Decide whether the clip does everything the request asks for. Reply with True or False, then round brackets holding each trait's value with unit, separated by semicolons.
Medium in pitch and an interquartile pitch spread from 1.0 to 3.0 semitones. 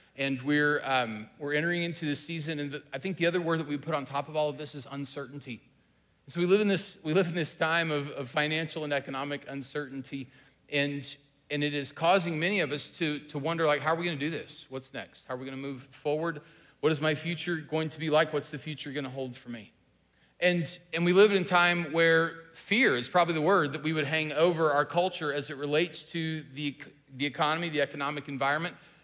True (150 Hz; 2.6 semitones)